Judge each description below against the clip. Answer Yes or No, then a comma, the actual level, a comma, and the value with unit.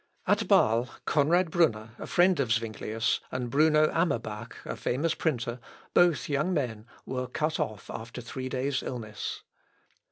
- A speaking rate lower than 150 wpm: Yes, average, 140 wpm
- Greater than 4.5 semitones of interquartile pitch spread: Yes, average, 5.2 semitones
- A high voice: No, low, 130 Hz